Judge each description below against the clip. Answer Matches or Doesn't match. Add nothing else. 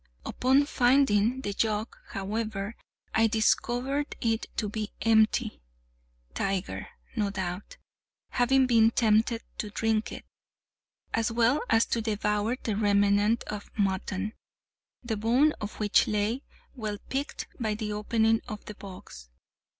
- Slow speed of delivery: Matches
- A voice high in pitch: Matches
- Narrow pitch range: Matches